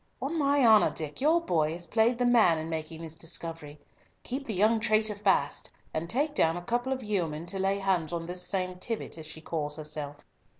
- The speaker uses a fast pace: Yes, fast, 210 wpm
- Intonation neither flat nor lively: No, wide, 6.0 semitones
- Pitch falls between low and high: Yes, medium, 180 Hz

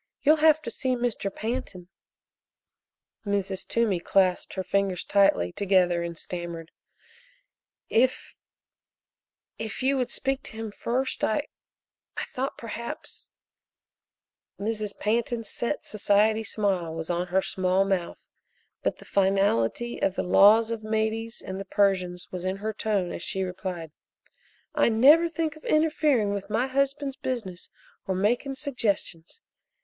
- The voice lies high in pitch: Yes, high, 210 Hz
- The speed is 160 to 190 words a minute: No, average, 140 wpm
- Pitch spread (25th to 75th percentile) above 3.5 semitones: Yes, average, 4.4 semitones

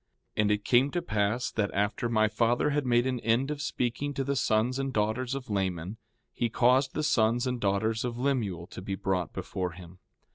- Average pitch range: Yes, average, 3.9 semitones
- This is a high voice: No, low, 115 Hz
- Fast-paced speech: Yes, fast, 210 wpm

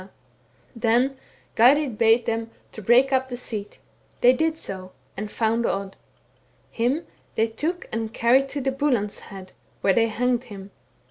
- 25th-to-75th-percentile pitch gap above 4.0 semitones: No, average, 3.2 semitones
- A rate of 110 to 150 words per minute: Yes, average, 145 wpm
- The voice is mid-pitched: No, high, 235 Hz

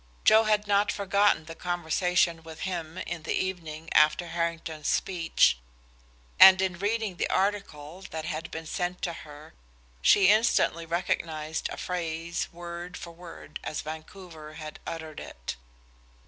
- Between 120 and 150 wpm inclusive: Yes, average, 140 wpm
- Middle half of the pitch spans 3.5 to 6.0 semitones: No, average, 2.8 semitones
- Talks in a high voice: No, medium, 170 Hz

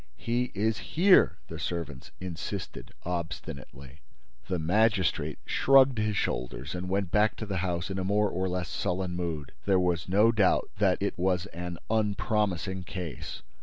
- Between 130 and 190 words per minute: Yes, average, 155 wpm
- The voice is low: Yes, very low, 90 Hz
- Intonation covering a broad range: No, average, 3.5 semitones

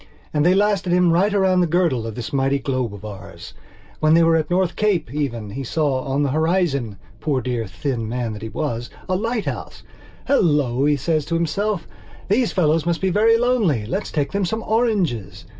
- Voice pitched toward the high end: No, medium, 155 Hz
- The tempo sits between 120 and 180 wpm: No, average, 195 wpm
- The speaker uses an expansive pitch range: Yes, wide, 6.7 semitones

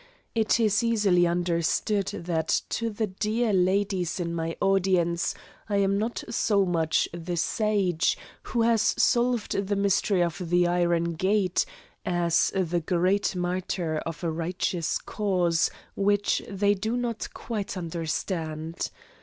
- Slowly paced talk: Yes, slow, 130 wpm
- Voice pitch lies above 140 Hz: Yes, medium, 185 Hz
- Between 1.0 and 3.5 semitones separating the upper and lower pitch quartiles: Yes, average, 3.2 semitones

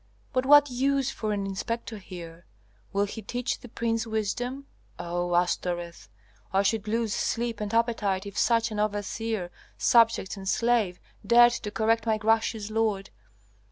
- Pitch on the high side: Yes, high, 220 Hz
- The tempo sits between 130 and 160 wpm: Yes, average, 150 wpm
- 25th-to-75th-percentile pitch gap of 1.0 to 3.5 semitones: Yes, average, 2.8 semitones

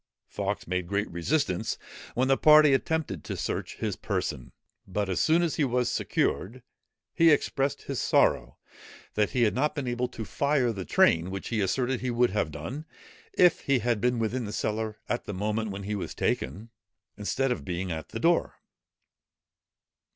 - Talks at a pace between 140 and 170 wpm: No, average, 180 wpm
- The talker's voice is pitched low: Yes, low, 115 Hz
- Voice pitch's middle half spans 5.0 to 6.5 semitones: Yes, wide, 5.5 semitones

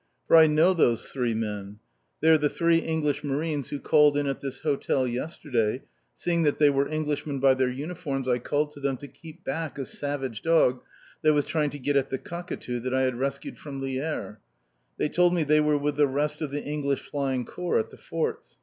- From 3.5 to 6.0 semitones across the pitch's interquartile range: No, narrow, 2.6 semitones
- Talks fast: Yes, fast, 215 wpm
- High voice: No, medium, 145 Hz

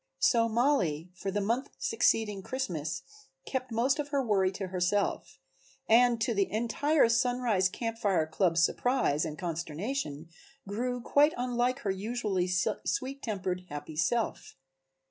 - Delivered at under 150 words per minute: Yes, slow, 135 wpm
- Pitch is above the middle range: Yes, high, 220 Hz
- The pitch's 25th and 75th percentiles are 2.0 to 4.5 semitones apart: No, wide, 5.4 semitones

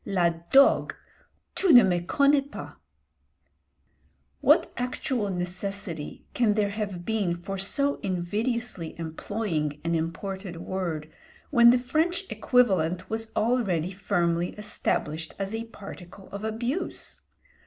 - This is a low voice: No, high, 200 Hz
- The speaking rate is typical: No, slow, 115 wpm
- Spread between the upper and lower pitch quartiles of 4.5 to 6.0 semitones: Yes, average, 5.1 semitones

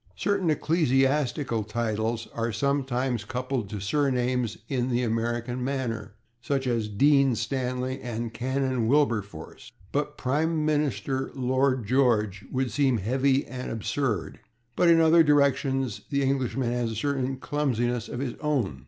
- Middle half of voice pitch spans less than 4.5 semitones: Yes, average, 3.1 semitones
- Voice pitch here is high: No, low, 130 Hz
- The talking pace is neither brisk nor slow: No, slow, 130 wpm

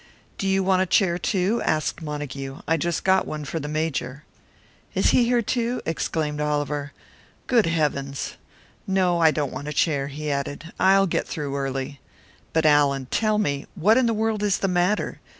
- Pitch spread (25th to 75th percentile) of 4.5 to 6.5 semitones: Yes, average, 5.0 semitones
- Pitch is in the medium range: Yes, medium, 160 Hz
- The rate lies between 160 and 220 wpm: Yes, average, 180 wpm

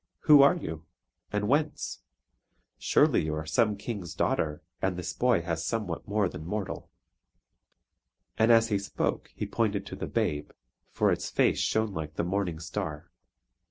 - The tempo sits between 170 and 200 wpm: No, average, 160 wpm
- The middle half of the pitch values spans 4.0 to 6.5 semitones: Yes, wide, 5.4 semitones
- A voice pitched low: Yes, low, 100 Hz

